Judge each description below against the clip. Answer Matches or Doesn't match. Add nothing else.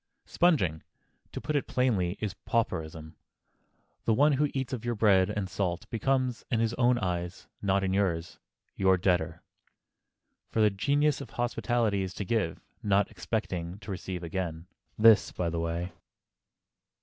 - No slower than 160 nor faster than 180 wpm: Doesn't match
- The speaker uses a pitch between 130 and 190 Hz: Doesn't match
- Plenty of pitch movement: Doesn't match